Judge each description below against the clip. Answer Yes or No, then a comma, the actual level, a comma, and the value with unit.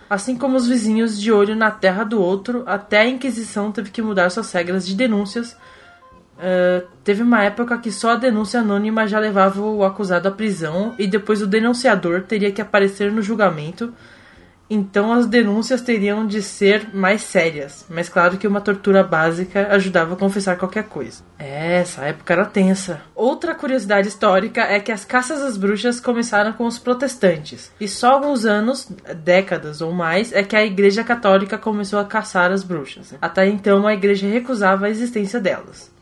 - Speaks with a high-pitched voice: Yes, high, 205 Hz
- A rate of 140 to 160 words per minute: No, average, 175 wpm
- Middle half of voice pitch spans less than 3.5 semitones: Yes, average, 3.1 semitones